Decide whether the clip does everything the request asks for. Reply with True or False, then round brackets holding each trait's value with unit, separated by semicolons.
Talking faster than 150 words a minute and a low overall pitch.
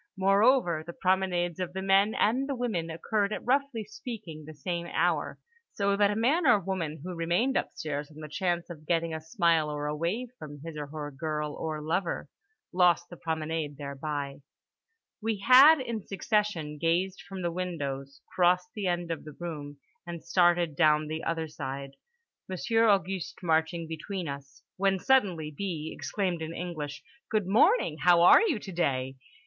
False (165 wpm; 170 Hz)